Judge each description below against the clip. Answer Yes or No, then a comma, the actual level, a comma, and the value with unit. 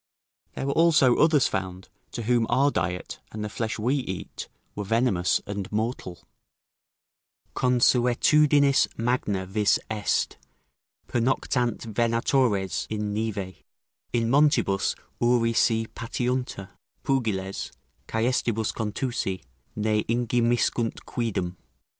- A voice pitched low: Yes, low, 115 Hz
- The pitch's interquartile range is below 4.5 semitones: Yes, average, 3.4 semitones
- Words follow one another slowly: Yes, slow, 100 wpm